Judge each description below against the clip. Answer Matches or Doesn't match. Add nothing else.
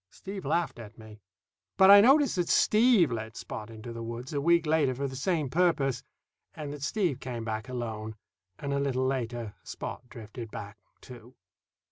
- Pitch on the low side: Matches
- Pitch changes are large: Matches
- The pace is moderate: Matches